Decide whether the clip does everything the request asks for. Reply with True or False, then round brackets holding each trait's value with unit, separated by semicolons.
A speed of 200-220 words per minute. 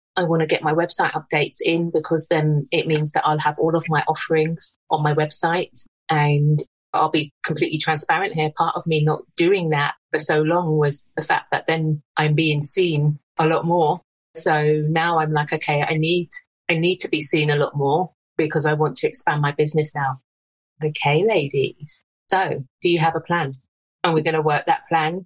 True (205 wpm)